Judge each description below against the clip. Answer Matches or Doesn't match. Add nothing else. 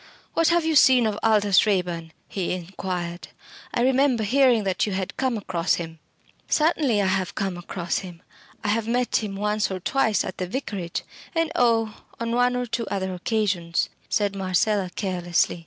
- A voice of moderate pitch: Doesn't match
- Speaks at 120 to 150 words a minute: Doesn't match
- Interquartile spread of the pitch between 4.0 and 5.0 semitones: Matches